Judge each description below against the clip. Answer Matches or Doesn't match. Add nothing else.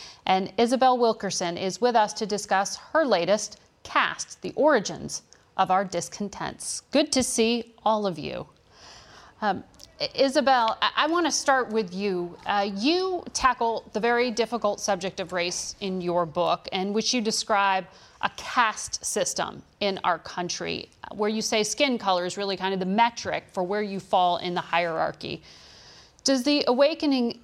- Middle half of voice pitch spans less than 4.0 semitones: Doesn't match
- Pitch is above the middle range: Matches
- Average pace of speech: Matches